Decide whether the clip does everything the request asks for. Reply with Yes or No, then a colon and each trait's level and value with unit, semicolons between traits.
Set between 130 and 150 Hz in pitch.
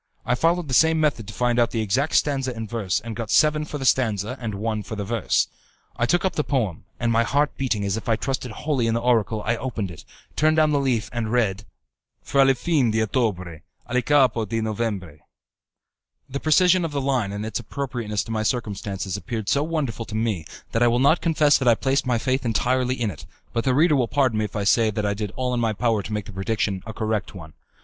No: low, 115 Hz